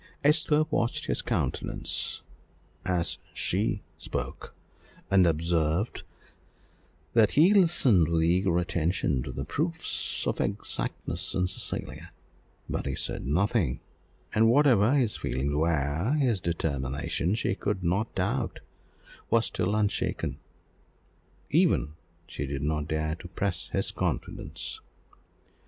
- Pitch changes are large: Yes, wide, 6.4 semitones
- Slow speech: Yes, slow, 115 wpm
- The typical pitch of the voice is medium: No, very low, 90 Hz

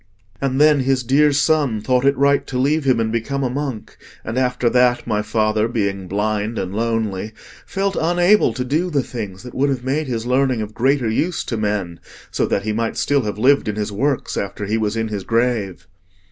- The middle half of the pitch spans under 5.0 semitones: Yes, average, 4.3 semitones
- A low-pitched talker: Yes, low, 120 Hz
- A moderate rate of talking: No, fast, 210 wpm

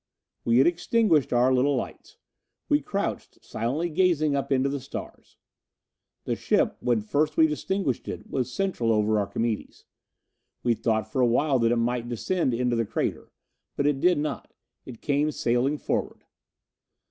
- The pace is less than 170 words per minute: Yes, average, 160 wpm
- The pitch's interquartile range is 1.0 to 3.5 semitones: No, average, 4.3 semitones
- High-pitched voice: No, low, 130 Hz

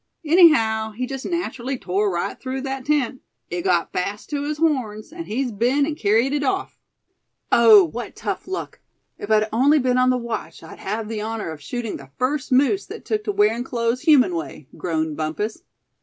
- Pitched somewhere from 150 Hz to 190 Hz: No, high, 240 Hz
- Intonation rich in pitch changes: No, average, 4.9 semitones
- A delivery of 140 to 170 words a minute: No, average, 190 wpm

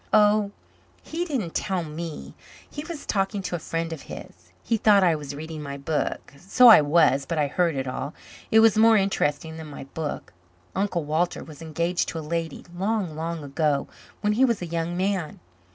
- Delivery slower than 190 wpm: No, average, 195 wpm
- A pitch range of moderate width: Yes, average, 4.8 semitones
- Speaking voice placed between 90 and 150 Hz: No, medium, 170 Hz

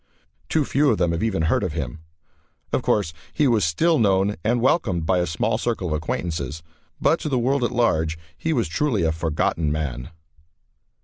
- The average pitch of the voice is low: Yes, very low, 95 Hz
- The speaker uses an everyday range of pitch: No, wide, 7.1 semitones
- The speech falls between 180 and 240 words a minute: Yes, average, 190 wpm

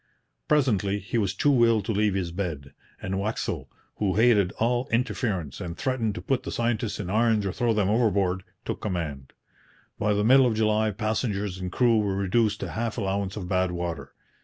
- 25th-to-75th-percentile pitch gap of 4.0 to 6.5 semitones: No, average, 3.5 semitones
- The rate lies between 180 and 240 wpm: Yes, average, 185 wpm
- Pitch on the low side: Yes, low, 105 Hz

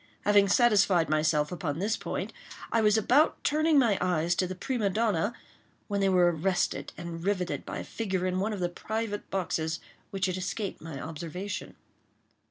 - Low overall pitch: No, high, 190 Hz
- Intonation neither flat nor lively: Yes, average, 3.3 semitones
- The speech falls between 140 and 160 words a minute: No, average, 175 wpm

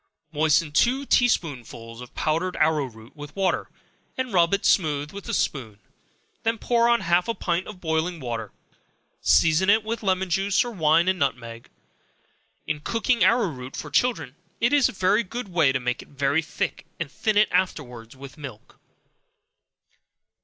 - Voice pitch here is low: No, medium, 165 Hz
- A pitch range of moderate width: No, wide, 6.4 semitones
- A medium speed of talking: Yes, average, 170 wpm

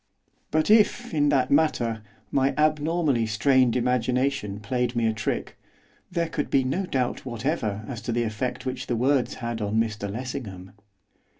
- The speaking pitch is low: Yes, low, 125 Hz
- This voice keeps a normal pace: Yes, average, 160 wpm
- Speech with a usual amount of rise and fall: Yes, average, 4.2 semitones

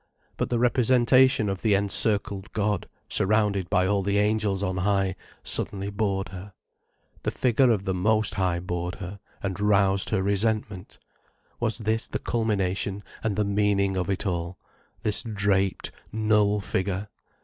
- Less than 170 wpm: Yes, average, 150 wpm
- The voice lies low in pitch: Yes, low, 100 Hz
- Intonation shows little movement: Yes, narrow, 2.0 semitones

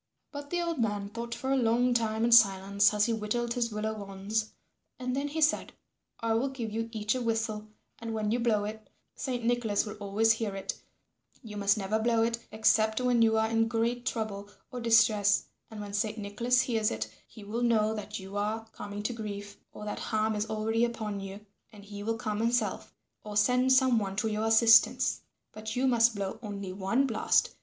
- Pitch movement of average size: No, narrow, 2.1 semitones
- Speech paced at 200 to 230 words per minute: Yes, fast, 205 wpm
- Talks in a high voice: Yes, high, 220 Hz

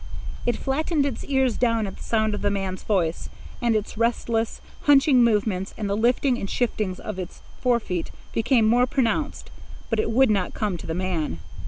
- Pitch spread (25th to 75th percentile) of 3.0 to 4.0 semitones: Yes, average, 3.7 semitones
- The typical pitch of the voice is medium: No, high, 225 Hz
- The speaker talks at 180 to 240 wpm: Yes, average, 185 wpm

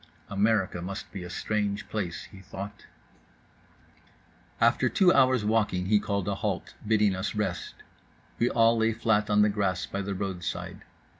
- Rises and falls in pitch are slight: Yes, narrow, 2.1 semitones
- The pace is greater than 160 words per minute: No, average, 155 wpm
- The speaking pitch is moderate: No, low, 100 Hz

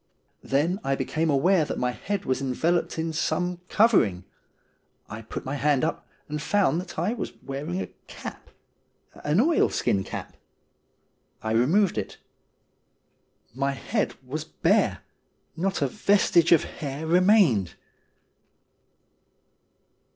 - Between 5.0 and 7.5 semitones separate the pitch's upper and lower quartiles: Yes, average, 5.3 semitones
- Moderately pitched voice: Yes, medium, 155 Hz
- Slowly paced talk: Yes, slow, 125 wpm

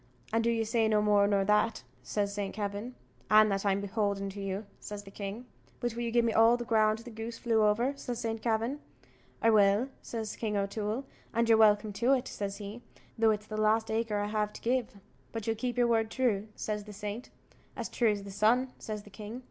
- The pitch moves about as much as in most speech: No, narrow, 2.0 semitones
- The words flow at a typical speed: No, fast, 225 wpm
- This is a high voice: Yes, high, 215 Hz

